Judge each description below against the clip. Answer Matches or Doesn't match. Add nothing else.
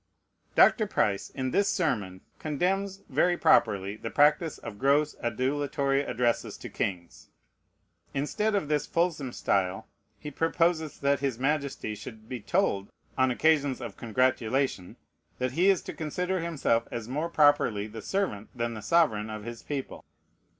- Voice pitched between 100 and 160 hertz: Matches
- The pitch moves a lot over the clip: Matches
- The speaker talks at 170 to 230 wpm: Doesn't match